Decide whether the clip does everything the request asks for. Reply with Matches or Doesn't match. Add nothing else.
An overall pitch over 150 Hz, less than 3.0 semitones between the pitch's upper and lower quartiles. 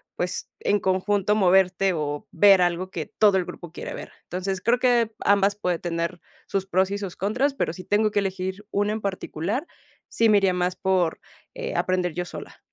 Matches